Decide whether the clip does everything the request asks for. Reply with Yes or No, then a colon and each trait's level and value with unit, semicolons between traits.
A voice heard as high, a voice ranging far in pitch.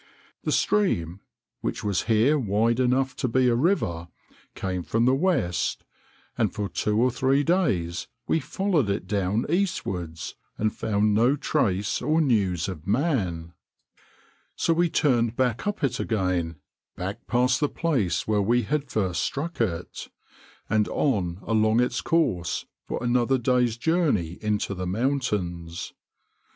No: low, 115 Hz; wide, 6.2 semitones